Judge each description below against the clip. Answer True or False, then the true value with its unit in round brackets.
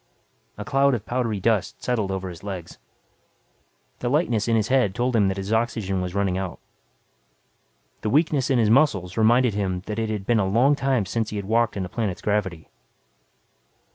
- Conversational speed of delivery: True (190 wpm)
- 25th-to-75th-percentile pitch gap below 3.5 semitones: False (3.9 semitones)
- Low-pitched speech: True (110 Hz)